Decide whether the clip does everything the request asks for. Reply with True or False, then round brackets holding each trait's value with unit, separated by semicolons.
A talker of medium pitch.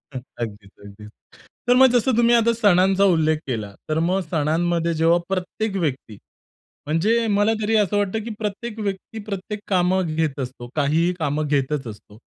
True (175 Hz)